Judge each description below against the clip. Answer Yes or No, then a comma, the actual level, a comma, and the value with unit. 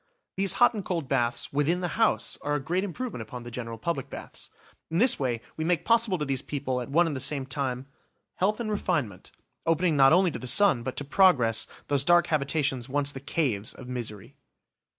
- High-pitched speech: No, medium, 145 Hz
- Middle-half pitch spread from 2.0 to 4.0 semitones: No, wide, 5.5 semitones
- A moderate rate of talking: No, fast, 210 wpm